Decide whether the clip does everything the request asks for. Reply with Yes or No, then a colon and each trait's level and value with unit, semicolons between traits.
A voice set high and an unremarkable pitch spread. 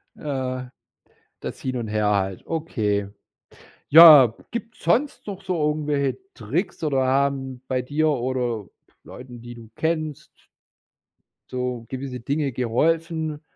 No: low, 130 Hz; average, 4.2 semitones